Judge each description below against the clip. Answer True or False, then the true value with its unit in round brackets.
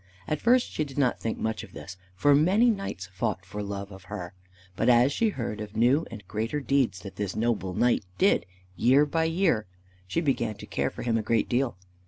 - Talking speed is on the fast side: True (215 wpm)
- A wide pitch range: True (5.9 semitones)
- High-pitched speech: False (120 Hz)